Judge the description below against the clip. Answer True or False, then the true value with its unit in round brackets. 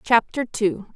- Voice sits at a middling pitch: False (215 Hz)